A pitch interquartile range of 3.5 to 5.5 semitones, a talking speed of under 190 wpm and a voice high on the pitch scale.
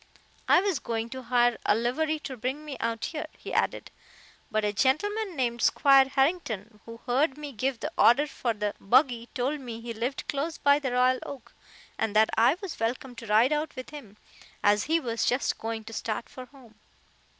No: average, 3.9 semitones; average, 195 wpm; very high, 250 Hz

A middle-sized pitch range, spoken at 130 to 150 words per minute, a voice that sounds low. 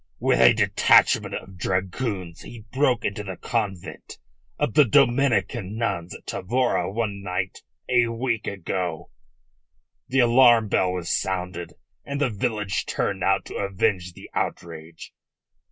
Yes: average, 4.5 semitones; slow, 135 wpm; low, 100 Hz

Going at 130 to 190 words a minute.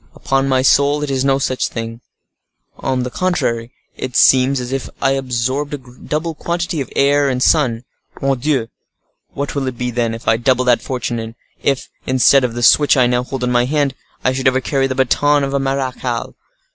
No: average, 200 wpm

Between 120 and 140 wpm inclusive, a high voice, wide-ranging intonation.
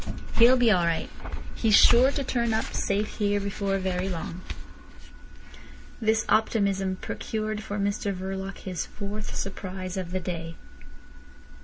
No: slow, 135 wpm; high, 200 Hz; narrow, 2.5 semitones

